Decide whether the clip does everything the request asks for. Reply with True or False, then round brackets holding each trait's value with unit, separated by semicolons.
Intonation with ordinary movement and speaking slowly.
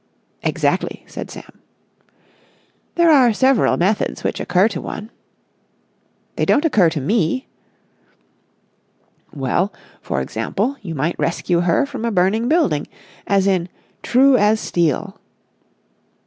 False (6.4 semitones; 120 wpm)